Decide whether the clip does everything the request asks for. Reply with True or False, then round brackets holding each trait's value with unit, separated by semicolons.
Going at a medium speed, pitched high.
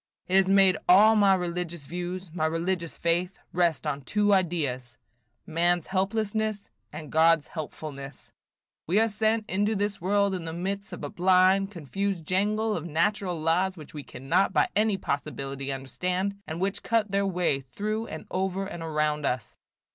False (165 wpm; 180 Hz)